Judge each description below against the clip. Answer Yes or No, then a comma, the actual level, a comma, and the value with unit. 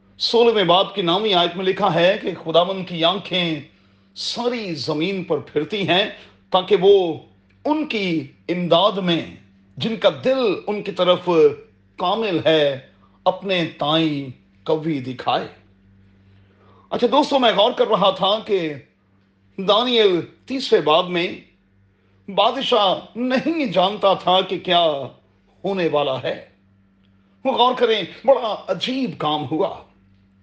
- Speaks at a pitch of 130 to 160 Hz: No, medium, 175 Hz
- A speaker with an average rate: Yes, average, 125 wpm